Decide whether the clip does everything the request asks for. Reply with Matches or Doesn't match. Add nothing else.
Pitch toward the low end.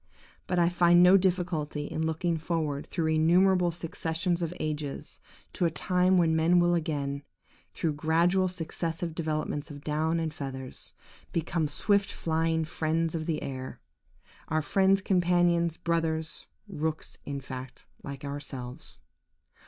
Doesn't match